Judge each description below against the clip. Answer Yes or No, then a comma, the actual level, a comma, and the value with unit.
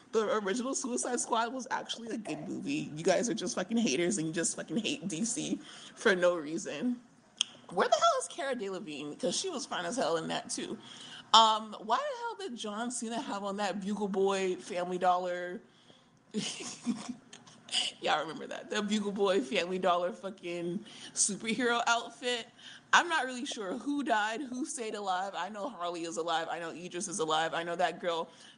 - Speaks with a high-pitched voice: Yes, high, 210 Hz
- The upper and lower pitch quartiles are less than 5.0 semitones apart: No, wide, 5.5 semitones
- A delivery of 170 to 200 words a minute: Yes, average, 185 wpm